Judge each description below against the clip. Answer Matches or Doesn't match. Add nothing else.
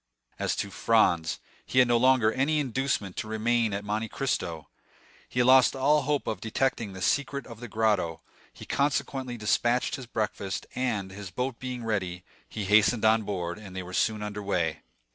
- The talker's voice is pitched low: Matches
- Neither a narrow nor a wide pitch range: Matches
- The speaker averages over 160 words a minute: Matches